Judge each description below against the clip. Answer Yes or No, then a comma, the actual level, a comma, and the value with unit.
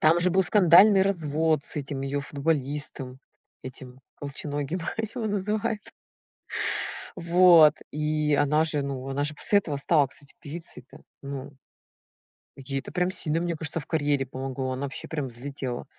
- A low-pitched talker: No, medium, 150 Hz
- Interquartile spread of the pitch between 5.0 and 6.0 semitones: No, average, 3.5 semitones